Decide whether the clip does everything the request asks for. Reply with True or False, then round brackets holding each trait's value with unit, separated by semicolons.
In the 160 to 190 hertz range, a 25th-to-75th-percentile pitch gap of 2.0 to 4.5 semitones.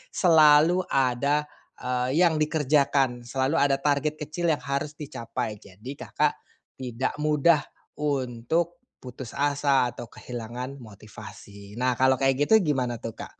False (135 Hz; 3.5 semitones)